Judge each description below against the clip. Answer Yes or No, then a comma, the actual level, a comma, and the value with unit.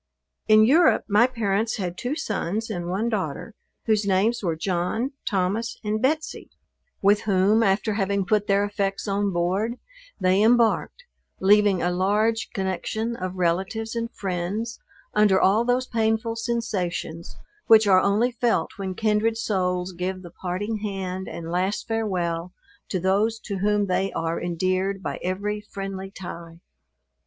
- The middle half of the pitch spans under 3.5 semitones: Yes, average, 3.1 semitones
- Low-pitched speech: No, high, 200 Hz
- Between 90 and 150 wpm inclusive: Yes, average, 145 wpm